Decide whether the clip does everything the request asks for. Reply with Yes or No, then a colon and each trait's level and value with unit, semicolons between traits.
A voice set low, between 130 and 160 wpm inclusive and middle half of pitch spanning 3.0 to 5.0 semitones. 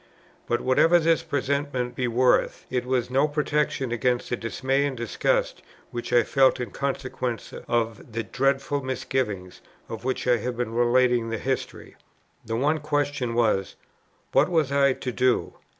No: low, 125 Hz; average, 155 wpm; narrow, 2.5 semitones